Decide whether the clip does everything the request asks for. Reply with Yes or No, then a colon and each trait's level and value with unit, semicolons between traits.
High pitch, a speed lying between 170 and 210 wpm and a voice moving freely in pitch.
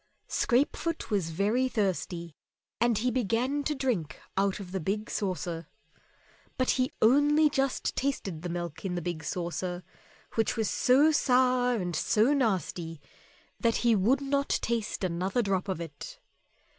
No: high, 215 Hz; average, 145 wpm; wide, 6.2 semitones